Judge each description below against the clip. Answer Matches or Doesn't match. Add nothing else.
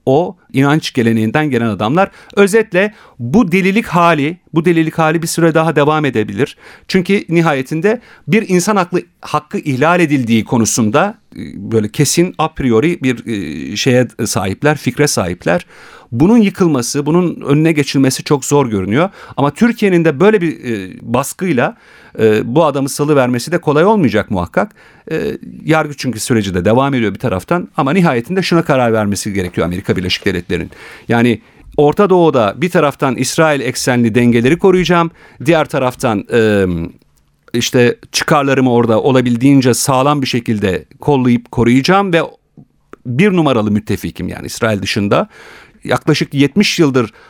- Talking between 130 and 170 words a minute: Matches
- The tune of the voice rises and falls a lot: Matches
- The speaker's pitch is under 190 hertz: Matches